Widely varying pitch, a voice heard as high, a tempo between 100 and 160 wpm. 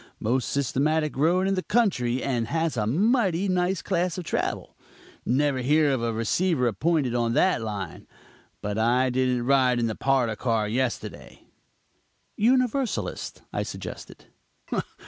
No: wide, 6.8 semitones; low, 135 Hz; average, 140 wpm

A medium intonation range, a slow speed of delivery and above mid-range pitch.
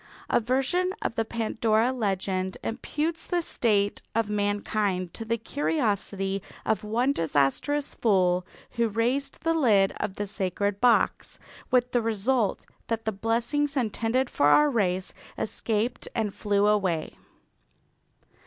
Yes: average, 3.8 semitones; slow, 130 wpm; high, 220 Hz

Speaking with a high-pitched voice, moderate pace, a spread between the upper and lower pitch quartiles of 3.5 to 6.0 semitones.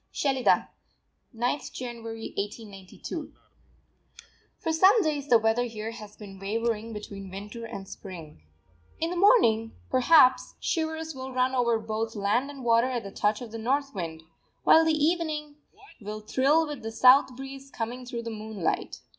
Yes: high, 235 Hz; average, 155 wpm; average, 4.3 semitones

